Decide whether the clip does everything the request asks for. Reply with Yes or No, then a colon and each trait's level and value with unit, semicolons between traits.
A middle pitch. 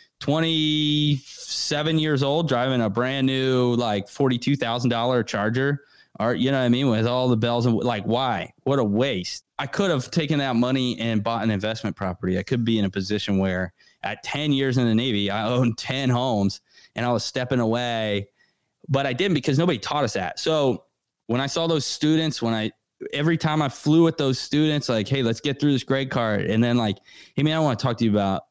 No: low, 125 Hz